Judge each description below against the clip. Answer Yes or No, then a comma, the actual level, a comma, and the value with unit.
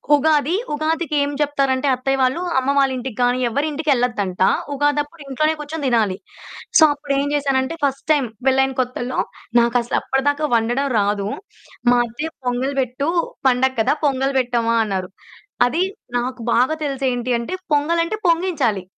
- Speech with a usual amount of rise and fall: Yes, average, 3.0 semitones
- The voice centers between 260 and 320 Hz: Yes, very high, 270 Hz